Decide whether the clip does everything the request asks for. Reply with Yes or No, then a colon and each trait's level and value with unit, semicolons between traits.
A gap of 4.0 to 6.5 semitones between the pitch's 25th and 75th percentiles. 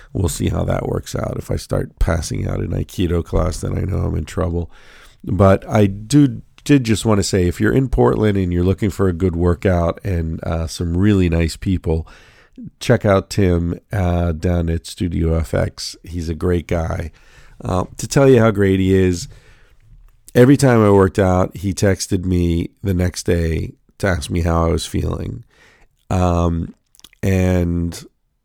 No: average, 3.4 semitones